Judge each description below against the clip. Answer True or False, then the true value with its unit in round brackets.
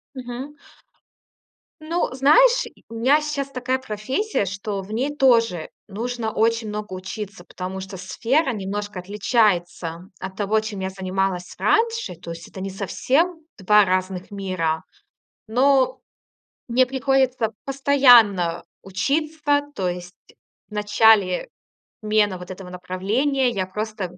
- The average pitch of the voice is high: True (210 Hz)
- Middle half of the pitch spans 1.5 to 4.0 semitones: False (5.6 semitones)